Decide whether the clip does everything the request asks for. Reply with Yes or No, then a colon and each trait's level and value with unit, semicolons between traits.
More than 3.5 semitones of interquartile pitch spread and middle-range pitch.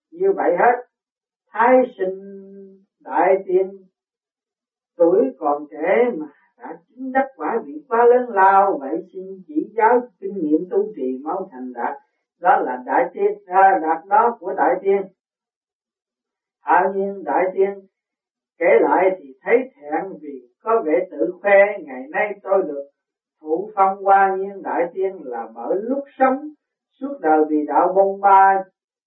No: average, 5.0 semitones; high, 195 Hz